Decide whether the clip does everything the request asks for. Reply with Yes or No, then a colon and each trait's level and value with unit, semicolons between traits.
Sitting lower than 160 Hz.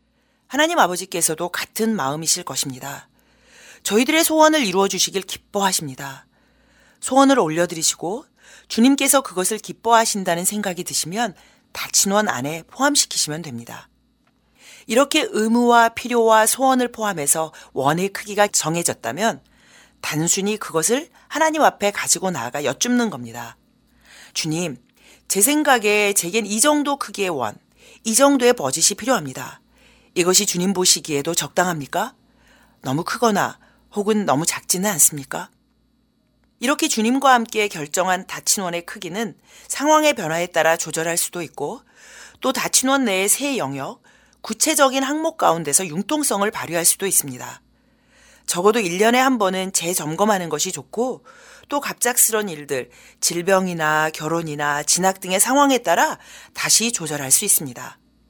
No: high, 205 Hz